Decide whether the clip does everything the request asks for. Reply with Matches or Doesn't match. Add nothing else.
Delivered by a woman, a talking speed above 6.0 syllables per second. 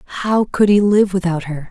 Doesn't match